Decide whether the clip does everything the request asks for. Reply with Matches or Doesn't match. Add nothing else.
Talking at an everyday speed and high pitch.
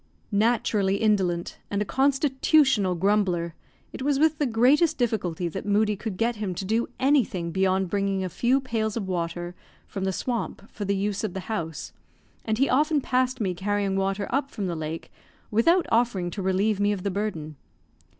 Matches